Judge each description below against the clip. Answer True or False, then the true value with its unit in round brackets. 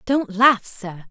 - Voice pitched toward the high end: True (220 Hz)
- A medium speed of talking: True (160 wpm)